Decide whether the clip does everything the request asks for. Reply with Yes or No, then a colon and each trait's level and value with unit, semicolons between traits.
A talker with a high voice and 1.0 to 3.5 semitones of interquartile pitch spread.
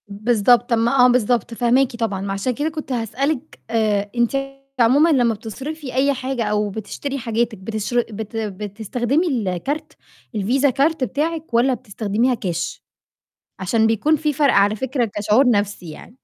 No: high, 235 Hz; average, 4.2 semitones